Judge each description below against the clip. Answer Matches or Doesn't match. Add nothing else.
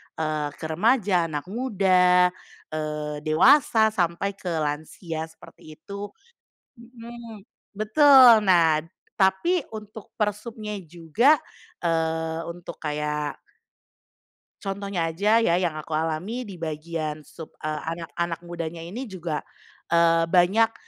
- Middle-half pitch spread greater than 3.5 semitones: Matches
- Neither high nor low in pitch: Matches